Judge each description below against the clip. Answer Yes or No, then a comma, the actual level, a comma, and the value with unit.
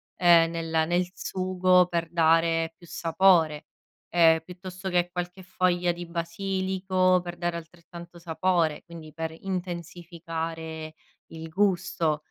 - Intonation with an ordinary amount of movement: No, narrow, 1.8 semitones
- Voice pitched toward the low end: No, medium, 170 Hz